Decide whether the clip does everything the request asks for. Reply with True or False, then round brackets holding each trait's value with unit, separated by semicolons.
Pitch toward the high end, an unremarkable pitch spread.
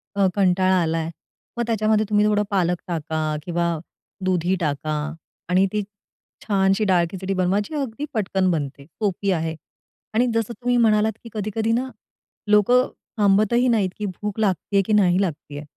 True (195 Hz; 3.3 semitones)